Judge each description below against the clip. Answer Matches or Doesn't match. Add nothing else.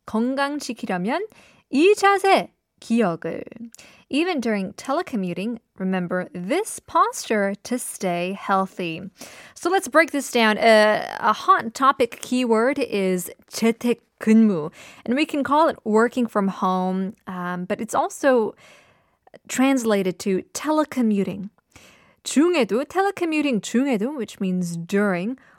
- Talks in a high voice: Matches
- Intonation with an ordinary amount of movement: Doesn't match